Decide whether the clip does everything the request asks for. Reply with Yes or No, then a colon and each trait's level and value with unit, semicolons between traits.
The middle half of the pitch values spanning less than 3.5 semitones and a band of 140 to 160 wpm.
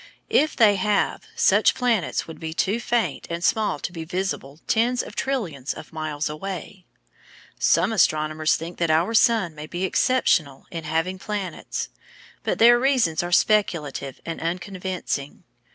No: wide, 5.4 semitones; average, 150 wpm